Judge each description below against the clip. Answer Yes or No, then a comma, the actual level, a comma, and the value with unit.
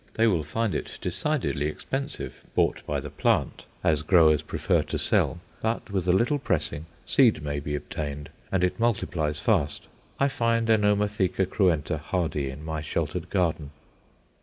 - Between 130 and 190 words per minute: Yes, average, 155 wpm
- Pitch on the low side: Yes, very low, 90 Hz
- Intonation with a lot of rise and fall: Yes, wide, 6.2 semitones